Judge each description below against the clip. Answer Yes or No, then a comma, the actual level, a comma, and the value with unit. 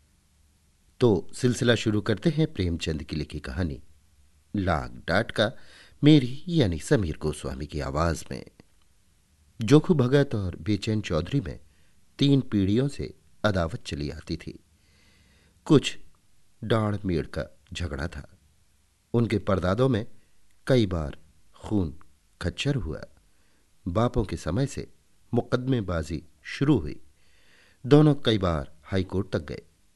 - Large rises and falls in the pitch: Yes, wide, 5.9 semitones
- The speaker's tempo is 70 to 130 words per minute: Yes, average, 120 wpm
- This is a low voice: Yes, very low, 90 Hz